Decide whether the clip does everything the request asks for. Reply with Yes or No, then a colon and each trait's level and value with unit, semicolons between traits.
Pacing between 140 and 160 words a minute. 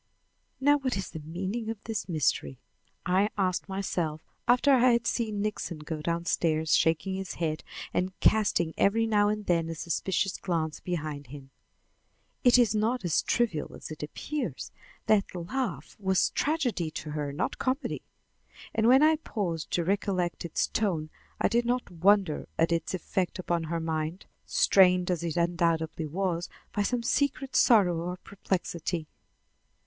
Yes: average, 155 wpm